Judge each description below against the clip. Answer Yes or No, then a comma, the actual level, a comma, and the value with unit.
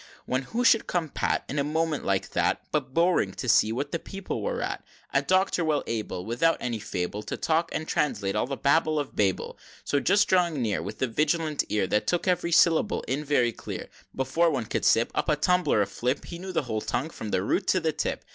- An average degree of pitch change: No, wide, 6.5 semitones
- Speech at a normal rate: No, fast, 235 wpm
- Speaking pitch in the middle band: Yes, medium, 145 Hz